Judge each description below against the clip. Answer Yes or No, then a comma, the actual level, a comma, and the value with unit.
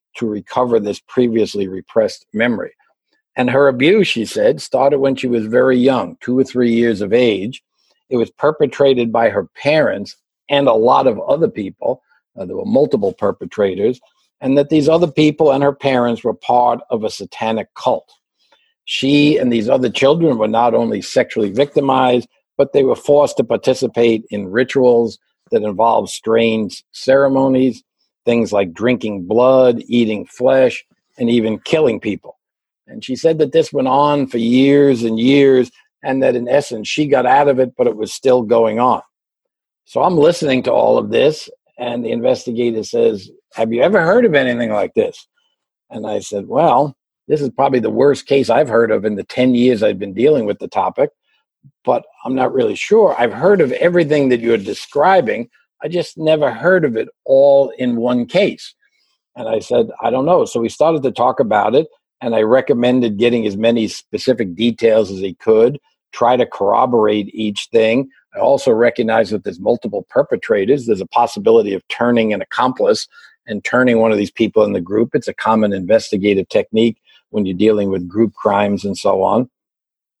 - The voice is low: Yes, low, 125 Hz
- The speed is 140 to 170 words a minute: No, average, 180 wpm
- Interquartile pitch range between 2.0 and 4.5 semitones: Yes, average, 3.9 semitones